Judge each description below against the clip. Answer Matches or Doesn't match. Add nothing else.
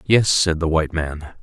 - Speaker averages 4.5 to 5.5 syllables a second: Matches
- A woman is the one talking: Doesn't match